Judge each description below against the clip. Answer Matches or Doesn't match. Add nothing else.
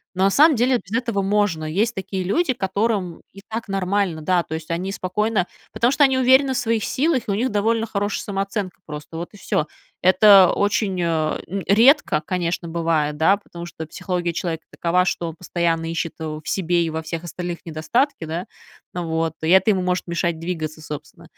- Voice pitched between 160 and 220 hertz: Matches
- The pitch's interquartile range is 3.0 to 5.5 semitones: Matches